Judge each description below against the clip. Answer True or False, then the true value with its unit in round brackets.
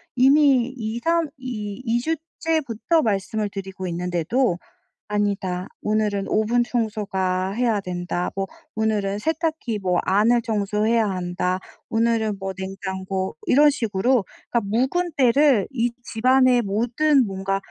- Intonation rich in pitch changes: False (4.3 semitones)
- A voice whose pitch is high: True (215 Hz)